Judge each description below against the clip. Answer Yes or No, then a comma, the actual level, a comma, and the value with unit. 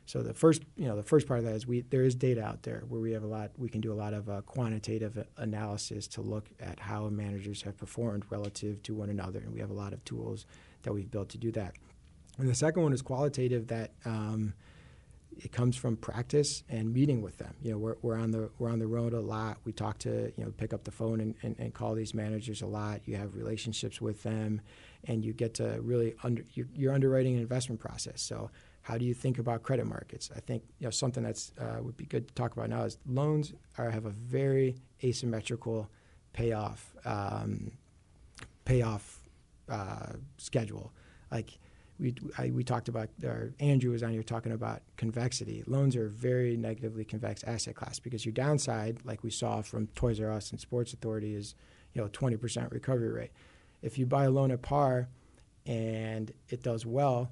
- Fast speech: Yes, fast, 210 wpm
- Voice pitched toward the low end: Yes, low, 115 Hz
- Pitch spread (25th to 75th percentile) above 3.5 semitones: No, narrow, 2.4 semitones